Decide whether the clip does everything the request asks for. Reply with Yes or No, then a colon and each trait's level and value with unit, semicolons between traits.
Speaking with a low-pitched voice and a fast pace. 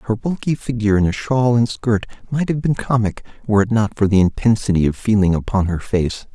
Yes: low, 110 Hz; fast, 220 wpm